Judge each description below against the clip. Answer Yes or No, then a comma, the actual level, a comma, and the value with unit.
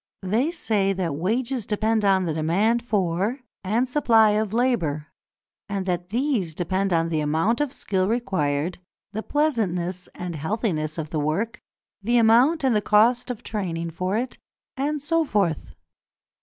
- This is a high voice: Yes, high, 205 Hz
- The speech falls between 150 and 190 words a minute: Yes, average, 155 wpm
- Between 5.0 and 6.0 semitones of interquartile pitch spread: Yes, wide, 5.5 semitones